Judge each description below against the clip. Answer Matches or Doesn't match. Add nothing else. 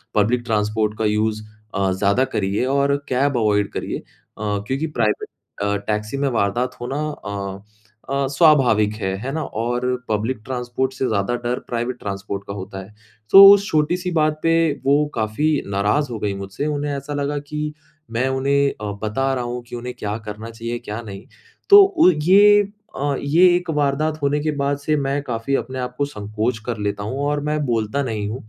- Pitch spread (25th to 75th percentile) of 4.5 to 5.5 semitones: Matches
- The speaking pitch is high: Doesn't match